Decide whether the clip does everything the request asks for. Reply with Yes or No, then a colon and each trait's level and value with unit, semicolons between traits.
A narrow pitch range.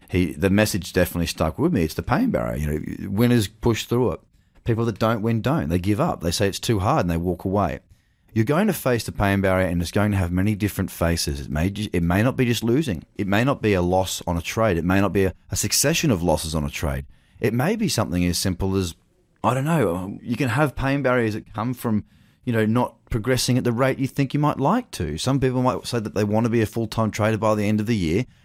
No: average, 4.5 semitones